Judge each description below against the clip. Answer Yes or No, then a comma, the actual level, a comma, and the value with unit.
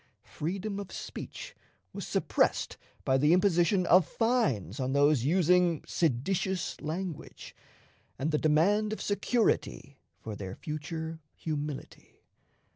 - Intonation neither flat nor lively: Yes, average, 4.6 semitones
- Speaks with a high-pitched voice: No, medium, 165 Hz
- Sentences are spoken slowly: Yes, slow, 115 wpm